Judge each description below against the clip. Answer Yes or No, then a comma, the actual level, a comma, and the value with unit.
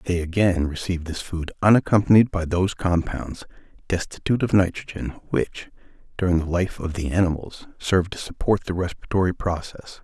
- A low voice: Yes, very low, 90 Hz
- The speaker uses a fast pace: No, average, 150 wpm